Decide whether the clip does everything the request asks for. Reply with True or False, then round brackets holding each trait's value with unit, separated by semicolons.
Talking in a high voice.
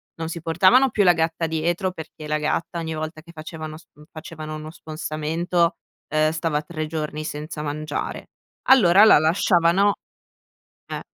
False (160 Hz)